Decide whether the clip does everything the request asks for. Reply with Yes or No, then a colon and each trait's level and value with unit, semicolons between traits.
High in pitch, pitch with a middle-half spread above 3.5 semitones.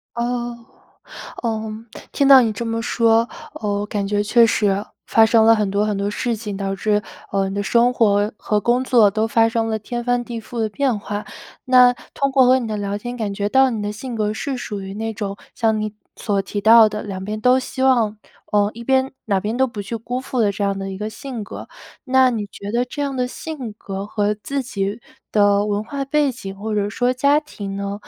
No: high, 220 Hz; average, 3.1 semitones